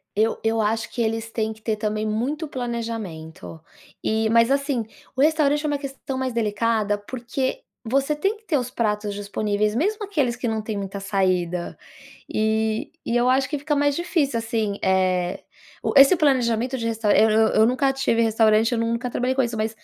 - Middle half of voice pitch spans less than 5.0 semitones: Yes, average, 3.8 semitones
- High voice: Yes, high, 230 Hz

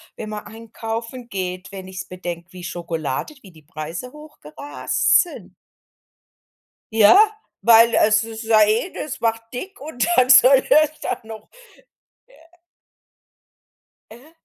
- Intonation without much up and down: No, average, 5.3 semitones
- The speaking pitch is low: No, high, 220 Hz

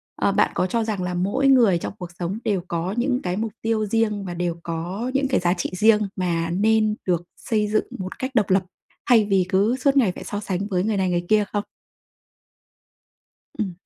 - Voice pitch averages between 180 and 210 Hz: Yes, high, 200 Hz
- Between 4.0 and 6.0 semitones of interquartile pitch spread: No, average, 3.6 semitones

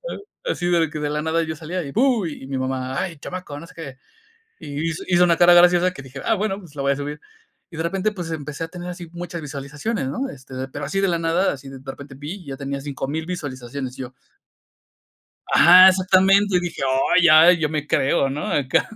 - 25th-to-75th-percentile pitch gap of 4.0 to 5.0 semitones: Yes, average, 4.3 semitones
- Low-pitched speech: No, medium, 160 Hz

